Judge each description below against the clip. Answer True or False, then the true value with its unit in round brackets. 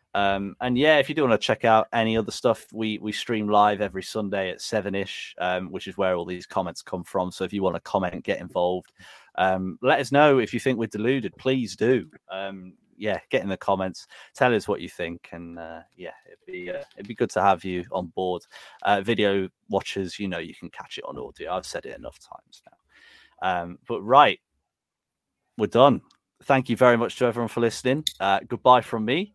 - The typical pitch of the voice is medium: False (105 Hz)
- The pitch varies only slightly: False (4.1 semitones)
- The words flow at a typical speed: False (225 wpm)